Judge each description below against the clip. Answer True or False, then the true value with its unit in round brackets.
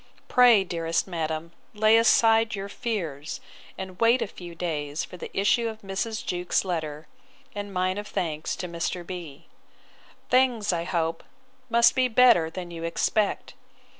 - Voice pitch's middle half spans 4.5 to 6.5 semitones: True (4.8 semitones)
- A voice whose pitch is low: False (185 Hz)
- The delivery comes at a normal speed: True (150 wpm)